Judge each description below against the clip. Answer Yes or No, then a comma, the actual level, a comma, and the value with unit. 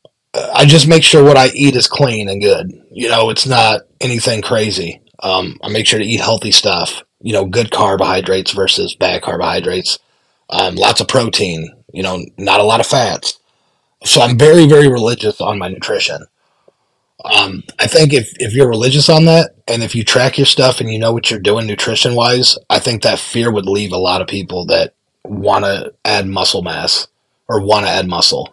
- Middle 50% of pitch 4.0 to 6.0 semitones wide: Yes, average, 4.7 semitones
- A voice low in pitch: Yes, low, 115 Hz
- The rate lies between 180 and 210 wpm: Yes, average, 200 wpm